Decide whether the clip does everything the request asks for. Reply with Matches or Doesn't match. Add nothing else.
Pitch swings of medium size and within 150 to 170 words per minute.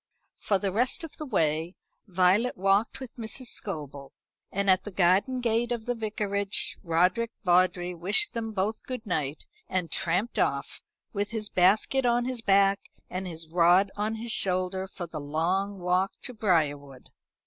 Matches